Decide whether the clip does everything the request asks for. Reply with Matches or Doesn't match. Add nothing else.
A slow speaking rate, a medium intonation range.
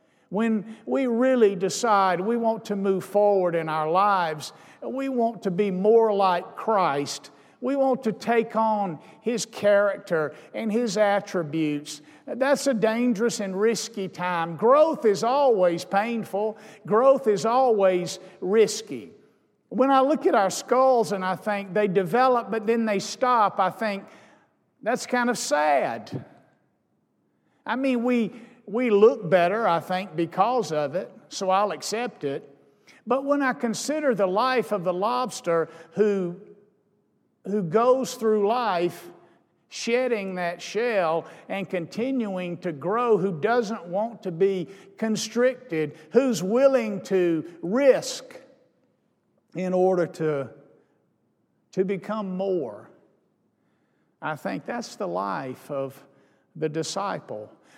Matches